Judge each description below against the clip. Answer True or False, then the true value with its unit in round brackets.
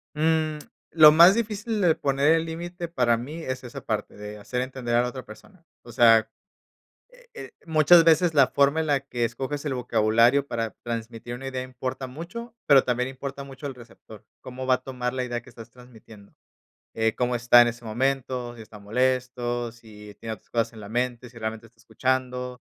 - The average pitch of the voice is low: True (125 Hz)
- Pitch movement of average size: True (3.3 semitones)